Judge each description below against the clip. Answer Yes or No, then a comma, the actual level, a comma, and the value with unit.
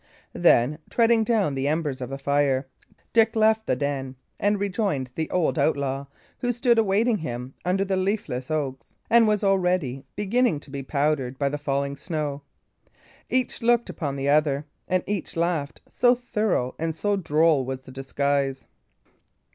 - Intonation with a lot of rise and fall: Yes, wide, 6.9 semitones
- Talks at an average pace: Yes, average, 160 wpm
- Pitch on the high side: No, medium, 155 Hz